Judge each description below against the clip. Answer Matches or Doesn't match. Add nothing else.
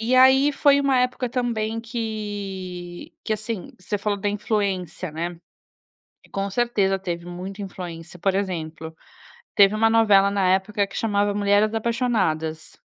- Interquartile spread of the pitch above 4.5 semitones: Doesn't match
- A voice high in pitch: Matches